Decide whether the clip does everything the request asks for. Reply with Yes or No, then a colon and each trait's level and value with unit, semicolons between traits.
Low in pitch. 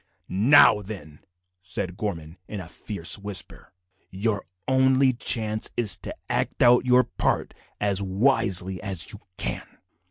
Yes: low, 100 Hz